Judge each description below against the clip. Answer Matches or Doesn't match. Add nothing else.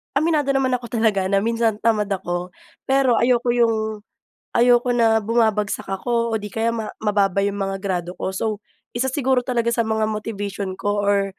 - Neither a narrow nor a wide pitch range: Matches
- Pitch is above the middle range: Matches